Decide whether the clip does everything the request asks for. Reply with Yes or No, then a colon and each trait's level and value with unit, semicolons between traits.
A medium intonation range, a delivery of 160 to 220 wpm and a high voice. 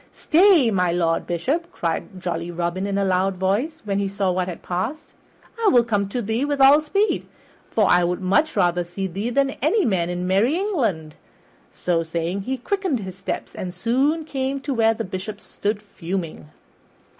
No: wide, 7.0 semitones; average, 180 wpm; high, 200 Hz